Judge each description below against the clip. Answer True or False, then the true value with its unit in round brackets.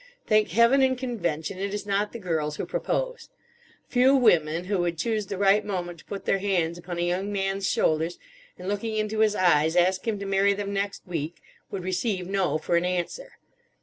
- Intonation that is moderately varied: True (3.4 semitones)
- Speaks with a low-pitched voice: False (195 Hz)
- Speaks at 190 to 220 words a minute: True (200 wpm)